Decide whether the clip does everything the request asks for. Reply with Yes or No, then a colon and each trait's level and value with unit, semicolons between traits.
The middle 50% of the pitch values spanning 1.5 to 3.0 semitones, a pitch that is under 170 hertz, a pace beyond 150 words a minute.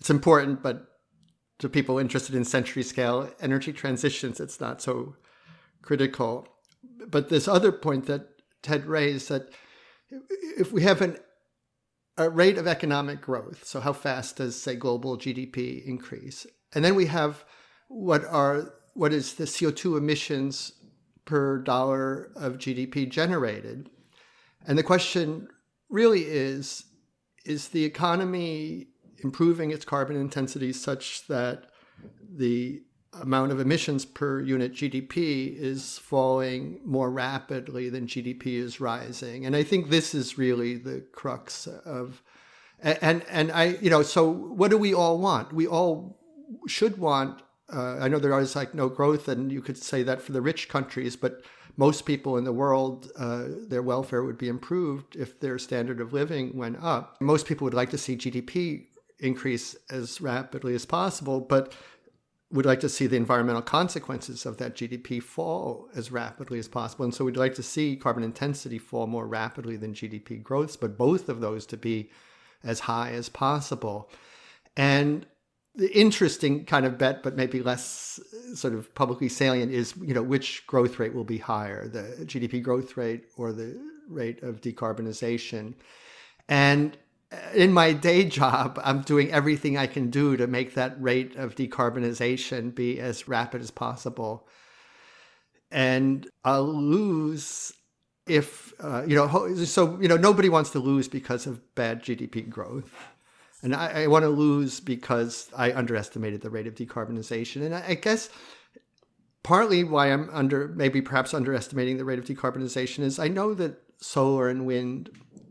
No: average, 3.5 semitones; low, 135 Hz; average, 160 wpm